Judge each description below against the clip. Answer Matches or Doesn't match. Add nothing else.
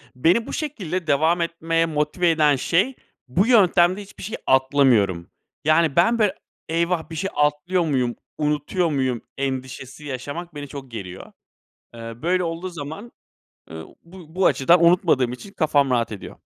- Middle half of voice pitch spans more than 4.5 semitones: Matches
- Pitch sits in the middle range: Matches